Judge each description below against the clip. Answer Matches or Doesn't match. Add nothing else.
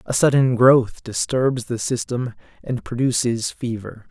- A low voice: Matches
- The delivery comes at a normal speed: Doesn't match